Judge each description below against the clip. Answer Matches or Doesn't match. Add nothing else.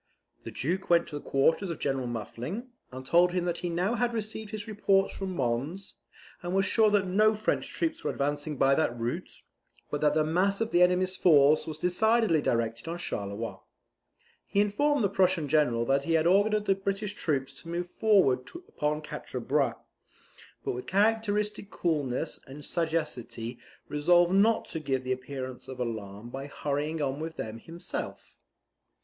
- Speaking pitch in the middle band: Matches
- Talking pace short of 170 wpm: Doesn't match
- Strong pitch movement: Matches